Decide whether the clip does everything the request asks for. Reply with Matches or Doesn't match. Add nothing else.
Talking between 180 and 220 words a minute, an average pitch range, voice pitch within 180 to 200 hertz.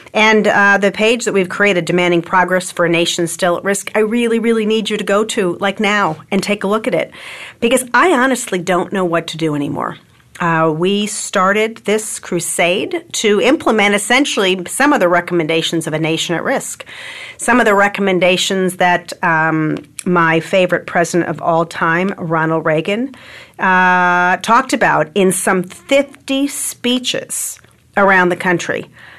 Doesn't match